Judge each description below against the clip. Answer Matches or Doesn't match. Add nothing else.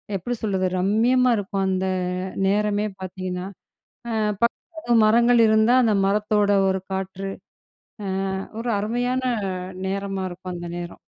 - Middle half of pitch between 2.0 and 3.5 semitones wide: Matches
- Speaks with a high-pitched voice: Matches